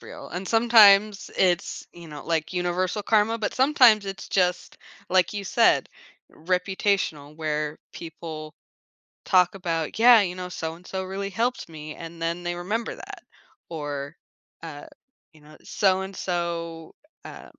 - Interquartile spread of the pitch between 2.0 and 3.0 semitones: No, average, 3.4 semitones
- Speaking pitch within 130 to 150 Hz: No, medium, 180 Hz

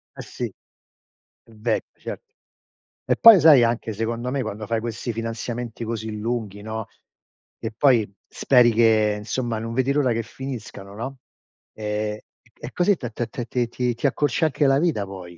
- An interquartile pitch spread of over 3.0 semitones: No, average, 2.7 semitones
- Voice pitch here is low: Yes, low, 115 Hz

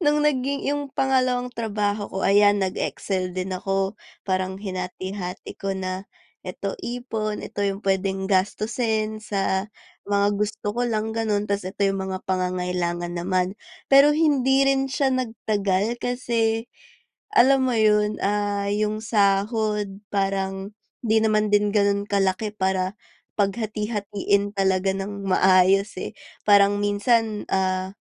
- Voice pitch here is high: Yes, high, 205 Hz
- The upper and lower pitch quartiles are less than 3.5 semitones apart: Yes, narrow, 2.5 semitones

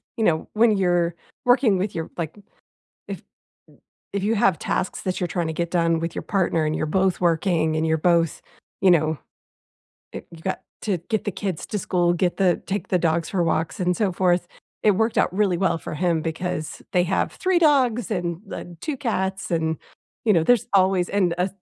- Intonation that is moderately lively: Yes, average, 3.1 semitones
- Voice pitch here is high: No, medium, 180 Hz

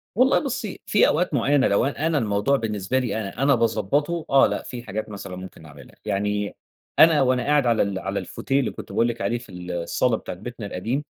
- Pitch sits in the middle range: No, low, 115 Hz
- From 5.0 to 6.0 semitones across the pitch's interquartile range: Yes, wide, 5.6 semitones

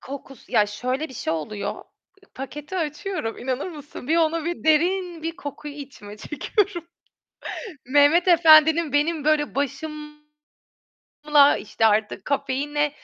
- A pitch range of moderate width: Yes, average, 3.3 semitones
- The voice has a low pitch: No, very high, 295 Hz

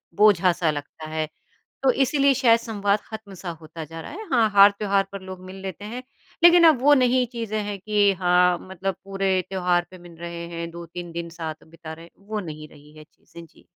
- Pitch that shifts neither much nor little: Yes, average, 4.1 semitones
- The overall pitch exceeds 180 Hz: Yes, high, 190 Hz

